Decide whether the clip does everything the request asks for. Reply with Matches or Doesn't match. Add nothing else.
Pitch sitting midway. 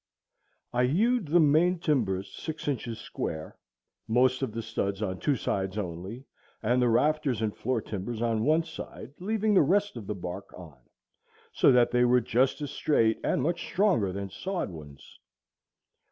Doesn't match